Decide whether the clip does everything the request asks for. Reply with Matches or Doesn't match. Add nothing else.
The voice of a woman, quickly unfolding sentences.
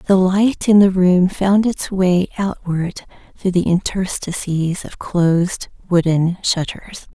Doesn't match